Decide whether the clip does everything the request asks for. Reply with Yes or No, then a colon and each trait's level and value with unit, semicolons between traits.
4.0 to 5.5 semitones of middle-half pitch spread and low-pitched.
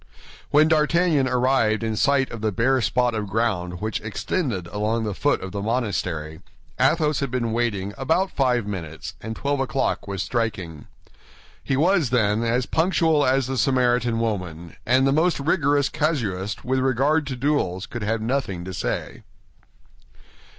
Yes: average, 4.9 semitones; low, 120 Hz